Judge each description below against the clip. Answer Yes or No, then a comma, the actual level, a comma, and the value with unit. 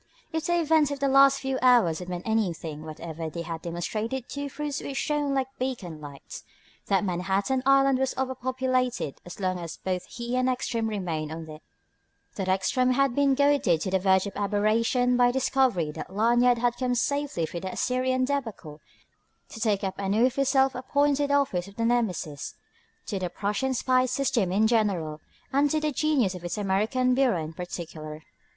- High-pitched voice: Yes, high, 230 Hz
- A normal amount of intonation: No, wide, 6.5 semitones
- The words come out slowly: No, average, 180 wpm